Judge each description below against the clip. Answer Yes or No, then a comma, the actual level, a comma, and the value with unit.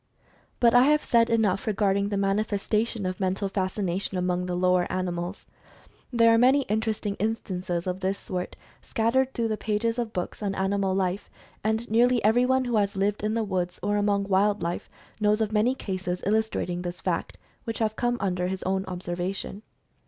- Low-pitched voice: No, high, 200 Hz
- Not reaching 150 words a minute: No, average, 175 wpm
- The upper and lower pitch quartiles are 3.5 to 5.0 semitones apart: No, average, 3.1 semitones